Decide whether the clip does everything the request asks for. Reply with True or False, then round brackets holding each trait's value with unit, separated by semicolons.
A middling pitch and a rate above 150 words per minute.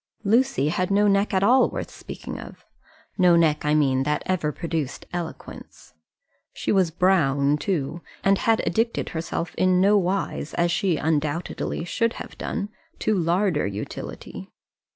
False (175 Hz; 145 wpm)